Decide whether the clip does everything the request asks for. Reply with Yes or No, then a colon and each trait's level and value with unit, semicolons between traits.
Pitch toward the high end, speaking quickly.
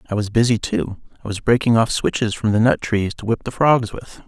No: low, 110 Hz; fast, 255 wpm